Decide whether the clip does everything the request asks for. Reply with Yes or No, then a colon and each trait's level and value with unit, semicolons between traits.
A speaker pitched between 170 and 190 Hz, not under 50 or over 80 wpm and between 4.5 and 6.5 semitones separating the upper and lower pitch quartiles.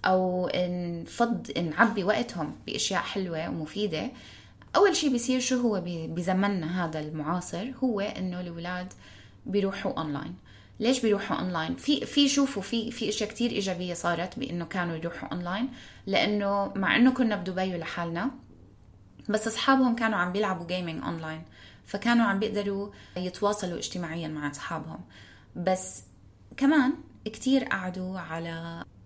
No: medium, 185 Hz; average, 130 wpm; average, 5.1 semitones